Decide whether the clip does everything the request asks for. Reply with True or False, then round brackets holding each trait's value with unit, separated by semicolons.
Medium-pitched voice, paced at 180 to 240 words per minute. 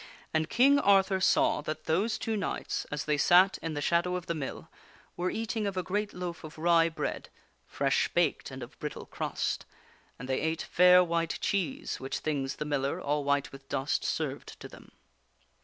True (170 Hz; 190 wpm)